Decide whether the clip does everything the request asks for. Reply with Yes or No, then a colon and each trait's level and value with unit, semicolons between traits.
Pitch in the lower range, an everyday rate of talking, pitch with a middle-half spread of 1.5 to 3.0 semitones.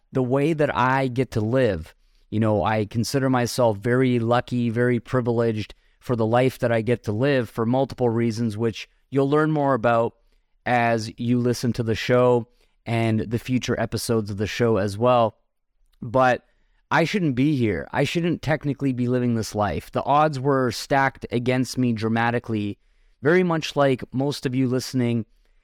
Yes: low, 120 Hz; average, 170 wpm; narrow, 2.4 semitones